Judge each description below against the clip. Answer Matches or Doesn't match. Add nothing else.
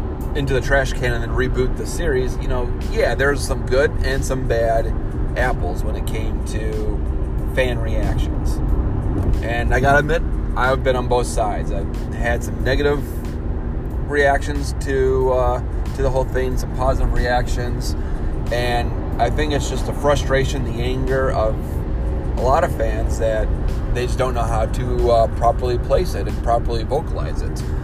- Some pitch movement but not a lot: Doesn't match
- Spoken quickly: Doesn't match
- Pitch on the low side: Matches